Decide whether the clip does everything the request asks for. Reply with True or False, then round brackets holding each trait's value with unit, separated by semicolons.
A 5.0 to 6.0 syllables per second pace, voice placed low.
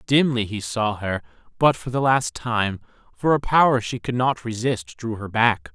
False (4.5 syllables/s; 115 Hz)